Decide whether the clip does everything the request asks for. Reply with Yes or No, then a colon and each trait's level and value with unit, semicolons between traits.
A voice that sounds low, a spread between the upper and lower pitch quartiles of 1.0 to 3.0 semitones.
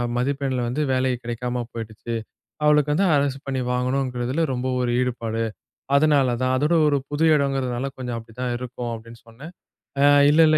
Yes: low, 130 Hz; narrow, 2.6 semitones